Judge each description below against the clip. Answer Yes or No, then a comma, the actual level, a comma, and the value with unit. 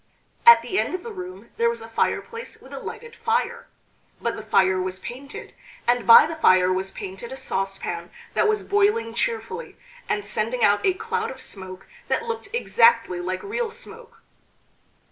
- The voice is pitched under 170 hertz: No, very high, 260 Hz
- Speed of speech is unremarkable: Yes, average, 175 wpm